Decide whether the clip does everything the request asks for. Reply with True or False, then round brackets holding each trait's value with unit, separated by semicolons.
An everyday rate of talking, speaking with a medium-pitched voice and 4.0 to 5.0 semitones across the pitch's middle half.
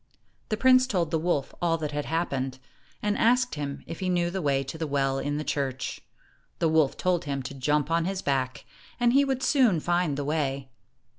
False (215 wpm; 160 Hz; 4.7 semitones)